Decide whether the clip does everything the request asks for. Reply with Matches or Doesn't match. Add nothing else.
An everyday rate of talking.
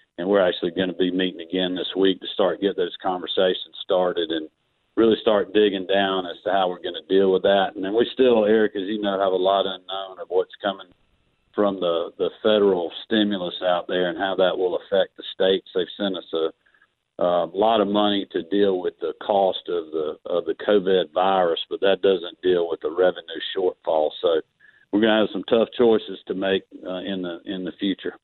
Doesn't match